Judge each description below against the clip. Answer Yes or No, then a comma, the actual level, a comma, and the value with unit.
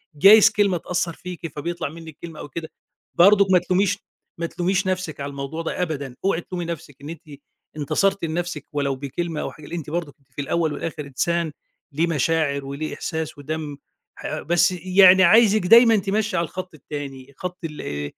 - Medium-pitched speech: Yes, medium, 165 Hz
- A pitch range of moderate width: Yes, average, 3.8 semitones